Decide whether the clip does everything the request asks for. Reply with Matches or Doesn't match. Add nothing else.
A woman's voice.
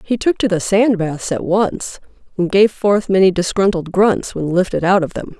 Matches